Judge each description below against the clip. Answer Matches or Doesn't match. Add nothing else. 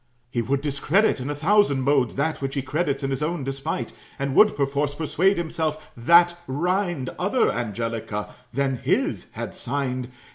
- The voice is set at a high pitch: Doesn't match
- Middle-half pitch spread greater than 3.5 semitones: Matches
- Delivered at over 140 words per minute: Matches